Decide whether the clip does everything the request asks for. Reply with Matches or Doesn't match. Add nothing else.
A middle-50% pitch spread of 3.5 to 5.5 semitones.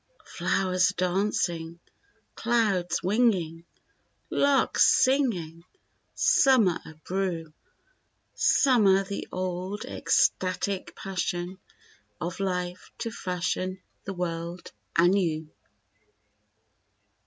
Doesn't match